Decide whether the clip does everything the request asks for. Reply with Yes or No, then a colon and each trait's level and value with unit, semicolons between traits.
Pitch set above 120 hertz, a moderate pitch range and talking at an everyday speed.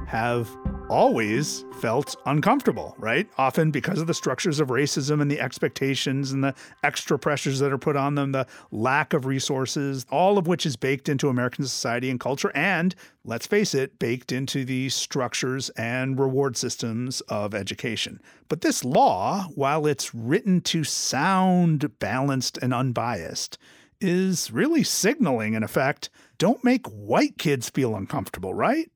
Yes: medium, 140 Hz; average, 4.0 semitones; average, 155 wpm